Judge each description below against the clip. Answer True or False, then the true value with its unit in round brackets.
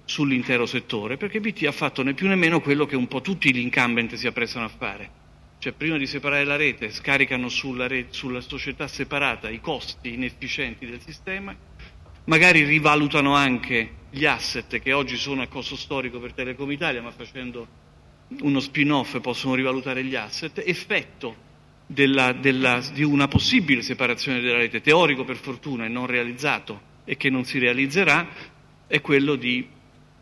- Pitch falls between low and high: False (130 Hz)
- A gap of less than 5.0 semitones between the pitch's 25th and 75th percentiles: True (2.7 semitones)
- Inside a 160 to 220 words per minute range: True (165 wpm)